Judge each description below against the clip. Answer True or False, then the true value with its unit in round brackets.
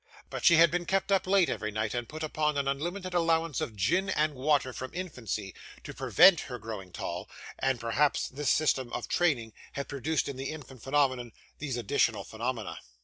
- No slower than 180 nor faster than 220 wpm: True (190 wpm)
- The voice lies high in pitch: False (140 Hz)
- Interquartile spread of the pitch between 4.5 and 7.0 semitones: True (5.2 semitones)